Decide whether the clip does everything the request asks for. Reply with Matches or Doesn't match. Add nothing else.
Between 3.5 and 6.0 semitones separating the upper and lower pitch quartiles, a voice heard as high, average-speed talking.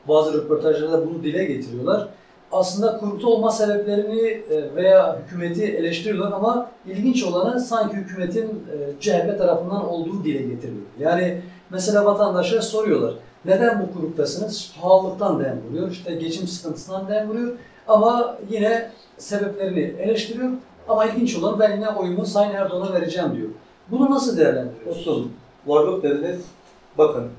Matches